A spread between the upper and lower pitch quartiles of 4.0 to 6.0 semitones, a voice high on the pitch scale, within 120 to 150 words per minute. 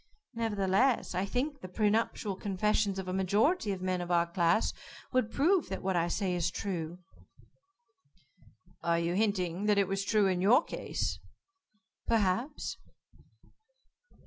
No: average, 3.2 semitones; high, 195 Hz; average, 145 wpm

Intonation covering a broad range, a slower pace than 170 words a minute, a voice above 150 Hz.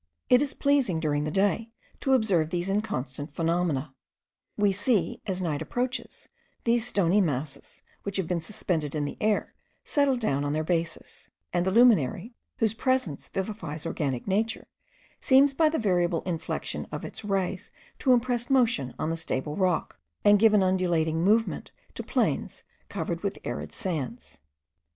Yes: wide, 6.0 semitones; average, 155 wpm; high, 190 Hz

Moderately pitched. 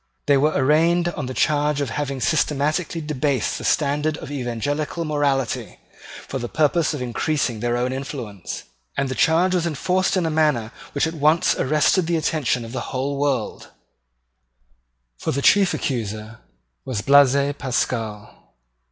Yes: medium, 145 Hz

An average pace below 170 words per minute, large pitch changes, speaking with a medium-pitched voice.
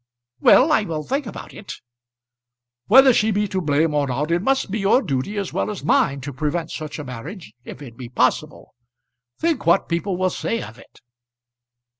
No: average, 190 wpm; wide, 6.6 semitones; medium, 170 Hz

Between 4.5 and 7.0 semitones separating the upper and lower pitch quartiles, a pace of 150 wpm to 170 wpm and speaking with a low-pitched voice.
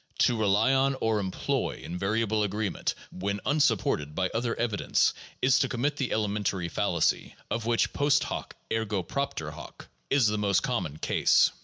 No: average, 3.8 semitones; average, 155 wpm; low, 105 Hz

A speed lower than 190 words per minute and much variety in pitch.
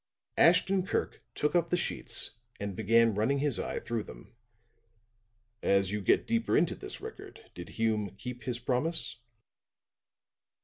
Yes: average, 140 wpm; wide, 7.5 semitones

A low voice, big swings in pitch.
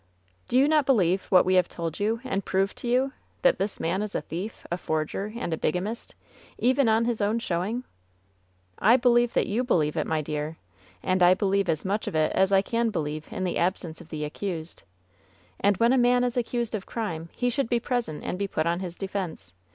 No: high, 195 Hz; wide, 5.8 semitones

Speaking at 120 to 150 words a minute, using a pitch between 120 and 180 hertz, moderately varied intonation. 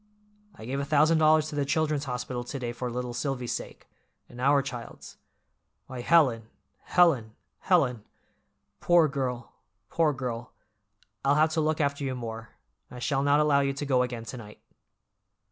No: average, 160 wpm; low, 135 Hz; average, 3.6 semitones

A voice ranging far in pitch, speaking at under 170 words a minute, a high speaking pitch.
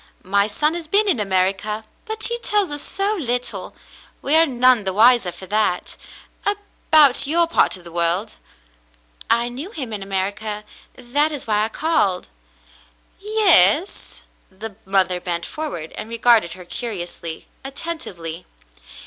Yes: wide, 8.6 semitones; average, 140 wpm; high, 230 Hz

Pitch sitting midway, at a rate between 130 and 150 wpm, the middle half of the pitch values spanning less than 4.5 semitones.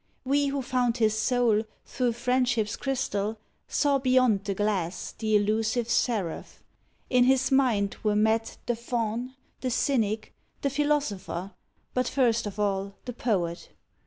No: high, 230 Hz; slow, 135 wpm; average, 3.4 semitones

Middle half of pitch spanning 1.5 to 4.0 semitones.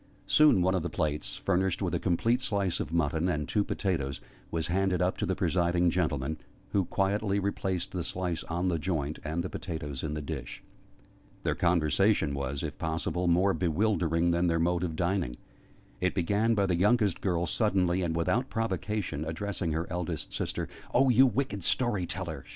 Yes: average, 3.3 semitones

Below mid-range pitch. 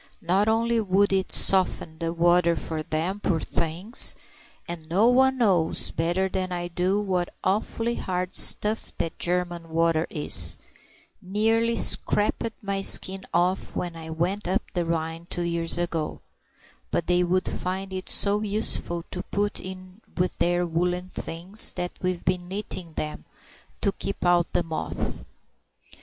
No: medium, 180 Hz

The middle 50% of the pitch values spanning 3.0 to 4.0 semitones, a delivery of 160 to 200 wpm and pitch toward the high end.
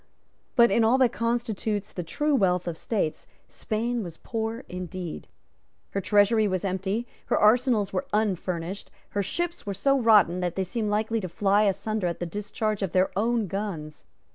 Yes: average, 3.6 semitones; average, 170 wpm; high, 205 Hz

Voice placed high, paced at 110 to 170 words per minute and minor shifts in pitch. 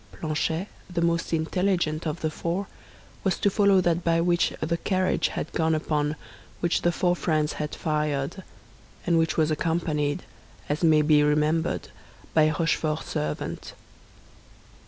No: medium, 160 Hz; average, 140 wpm; narrow, 2.2 semitones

